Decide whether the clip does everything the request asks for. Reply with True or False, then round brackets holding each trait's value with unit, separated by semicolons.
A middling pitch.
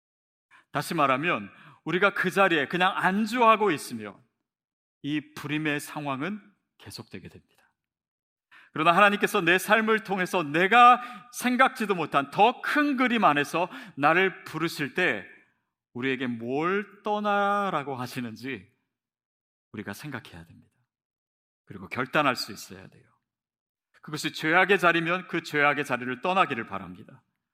True (170 Hz)